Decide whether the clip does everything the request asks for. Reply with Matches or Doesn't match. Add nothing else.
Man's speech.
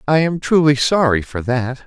Matches